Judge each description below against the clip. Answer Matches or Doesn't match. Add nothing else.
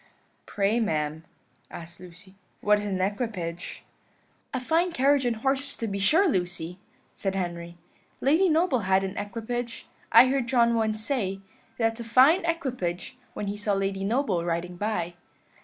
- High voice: Matches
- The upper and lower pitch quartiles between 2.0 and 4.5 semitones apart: Doesn't match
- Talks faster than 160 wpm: Doesn't match